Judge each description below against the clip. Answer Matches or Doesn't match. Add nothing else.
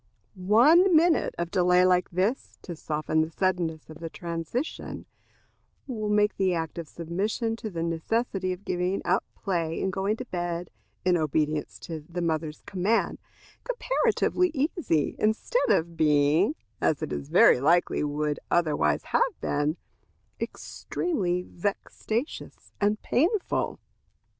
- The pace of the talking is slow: Matches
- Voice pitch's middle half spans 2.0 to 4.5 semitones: Doesn't match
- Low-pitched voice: Doesn't match